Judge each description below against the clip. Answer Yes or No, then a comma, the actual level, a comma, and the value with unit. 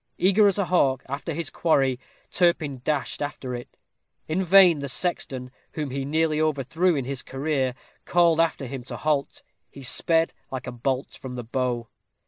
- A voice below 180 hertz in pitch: Yes, medium, 140 Hz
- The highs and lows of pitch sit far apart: No, average, 4.0 semitones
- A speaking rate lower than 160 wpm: No, average, 170 wpm